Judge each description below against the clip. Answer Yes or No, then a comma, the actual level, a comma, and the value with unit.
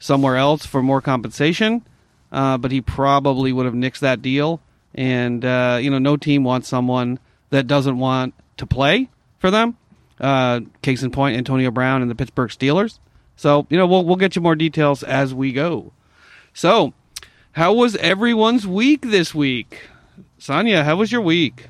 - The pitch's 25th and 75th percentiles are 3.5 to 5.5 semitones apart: Yes, average, 3.9 semitones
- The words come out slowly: No, average, 175 wpm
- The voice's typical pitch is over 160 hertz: No, low, 135 Hz